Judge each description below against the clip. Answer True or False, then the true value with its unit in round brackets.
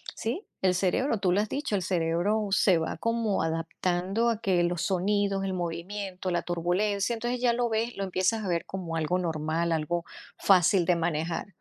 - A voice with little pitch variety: False (3.4 semitones)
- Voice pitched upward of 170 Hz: True (185 Hz)